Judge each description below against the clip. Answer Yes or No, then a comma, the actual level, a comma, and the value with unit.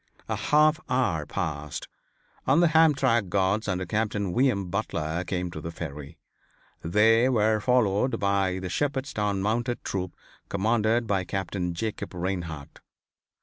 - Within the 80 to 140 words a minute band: Yes, slow, 135 wpm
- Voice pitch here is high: No, low, 100 Hz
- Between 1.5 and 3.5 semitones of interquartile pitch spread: No, average, 4.7 semitones